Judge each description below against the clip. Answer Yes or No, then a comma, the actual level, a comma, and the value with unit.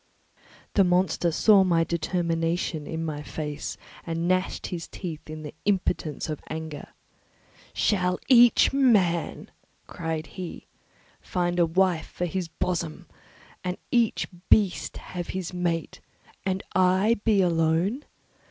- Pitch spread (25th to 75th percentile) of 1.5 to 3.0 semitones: Yes, narrow, 2.5 semitones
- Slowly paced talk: Yes, slow, 125 wpm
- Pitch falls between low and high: Yes, medium, 175 Hz